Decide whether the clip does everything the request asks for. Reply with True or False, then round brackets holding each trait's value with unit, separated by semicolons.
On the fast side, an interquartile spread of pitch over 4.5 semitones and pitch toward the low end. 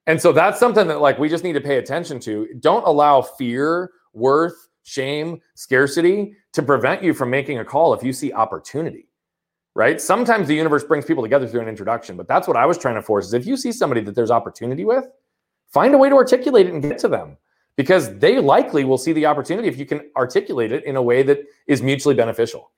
False (230 wpm; 5.2 semitones; 145 Hz)